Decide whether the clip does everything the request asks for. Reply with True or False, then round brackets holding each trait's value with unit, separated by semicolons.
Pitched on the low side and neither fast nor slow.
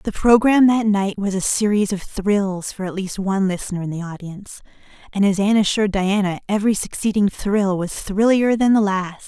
False (200 Hz; 195 wpm)